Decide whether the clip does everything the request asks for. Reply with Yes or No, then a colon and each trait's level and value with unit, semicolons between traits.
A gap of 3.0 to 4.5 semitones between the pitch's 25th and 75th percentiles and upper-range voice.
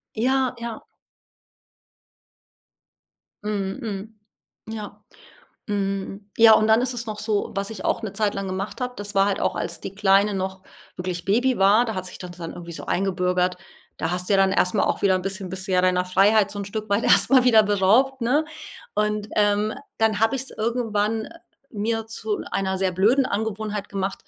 No: narrow, 2.5 semitones; high, 205 Hz